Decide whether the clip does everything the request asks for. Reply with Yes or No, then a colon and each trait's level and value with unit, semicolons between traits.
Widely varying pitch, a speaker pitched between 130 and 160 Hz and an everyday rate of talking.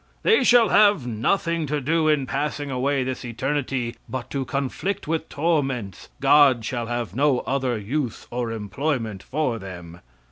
No: average, 4.1 semitones; low, 135 Hz; average, 150 wpm